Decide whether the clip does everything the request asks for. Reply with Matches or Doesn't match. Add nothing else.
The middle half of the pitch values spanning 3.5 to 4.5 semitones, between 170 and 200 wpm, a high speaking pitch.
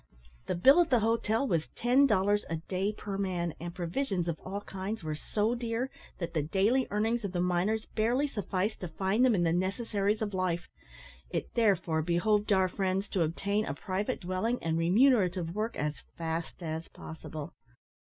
Matches